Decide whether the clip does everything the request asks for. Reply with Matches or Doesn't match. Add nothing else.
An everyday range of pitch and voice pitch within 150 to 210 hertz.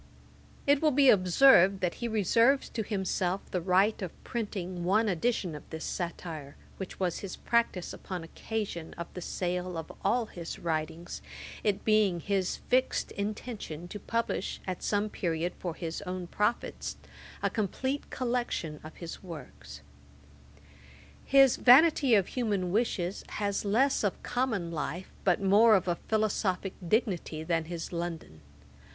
Matches